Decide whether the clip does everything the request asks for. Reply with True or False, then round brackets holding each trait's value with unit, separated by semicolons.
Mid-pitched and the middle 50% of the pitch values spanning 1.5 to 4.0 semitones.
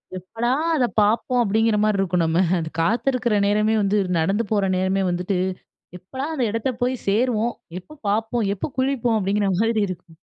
False (210 Hz; 3.7 semitones)